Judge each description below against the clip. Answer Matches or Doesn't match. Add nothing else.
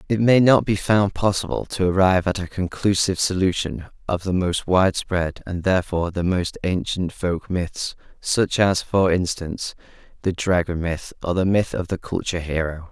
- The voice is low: Matches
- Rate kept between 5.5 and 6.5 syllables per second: Doesn't match